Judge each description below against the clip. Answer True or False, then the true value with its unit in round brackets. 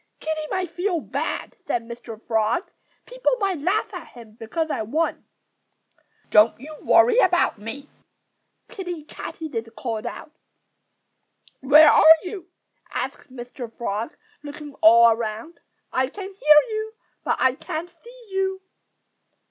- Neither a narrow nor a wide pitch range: False (7.8 semitones)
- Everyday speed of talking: False (130 wpm)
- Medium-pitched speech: False (305 Hz)